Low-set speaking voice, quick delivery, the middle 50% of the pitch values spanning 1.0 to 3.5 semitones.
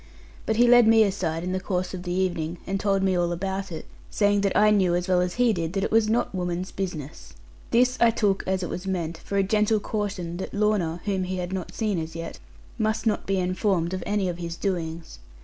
No: high, 190 Hz; fast, 235 wpm; average, 2.9 semitones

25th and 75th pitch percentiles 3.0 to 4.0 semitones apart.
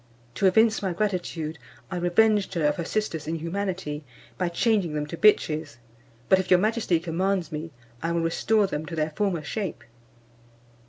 Yes: average, 3.7 semitones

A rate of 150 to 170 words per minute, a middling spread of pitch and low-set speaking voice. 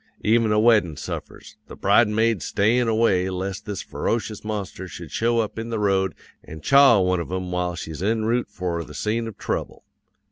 No: average, 185 wpm; average, 3.7 semitones; low, 105 Hz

